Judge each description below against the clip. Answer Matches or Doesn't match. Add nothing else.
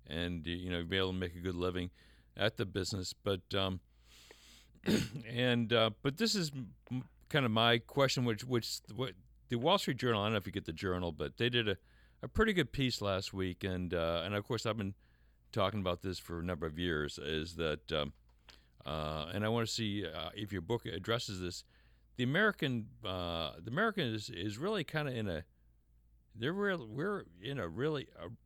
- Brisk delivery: Matches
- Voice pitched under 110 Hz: Matches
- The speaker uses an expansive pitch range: Matches